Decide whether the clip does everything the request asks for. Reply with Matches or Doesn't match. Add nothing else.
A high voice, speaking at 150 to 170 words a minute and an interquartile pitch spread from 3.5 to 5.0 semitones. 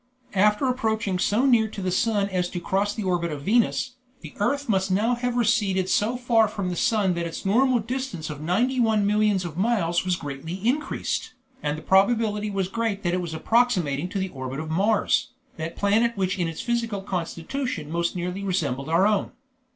Doesn't match